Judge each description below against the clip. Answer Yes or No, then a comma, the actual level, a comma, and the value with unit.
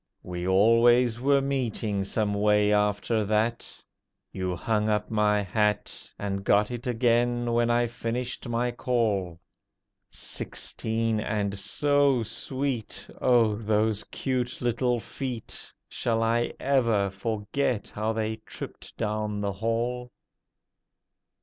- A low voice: Yes, low, 110 Hz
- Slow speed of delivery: Yes, slow, 115 wpm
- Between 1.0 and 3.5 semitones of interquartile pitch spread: Yes, narrow, 2.5 semitones